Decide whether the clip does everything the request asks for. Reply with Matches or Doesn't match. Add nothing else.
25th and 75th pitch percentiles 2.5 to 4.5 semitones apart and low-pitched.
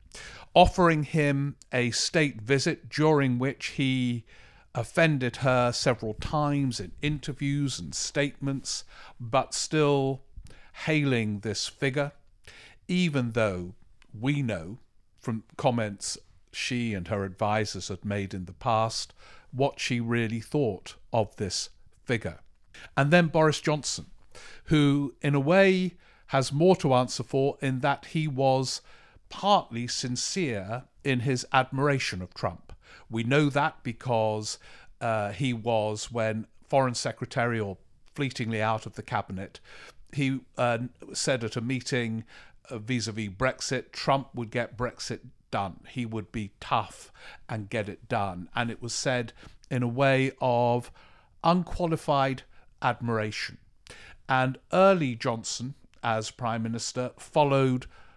Matches